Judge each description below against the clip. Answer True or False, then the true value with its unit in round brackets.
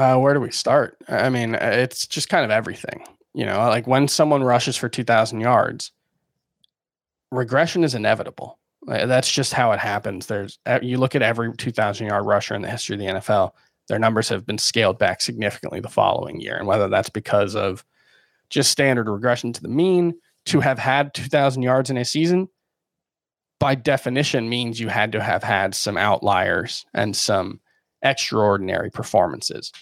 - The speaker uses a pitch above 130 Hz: False (125 Hz)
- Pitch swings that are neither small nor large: True (3.3 semitones)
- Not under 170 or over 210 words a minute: True (175 wpm)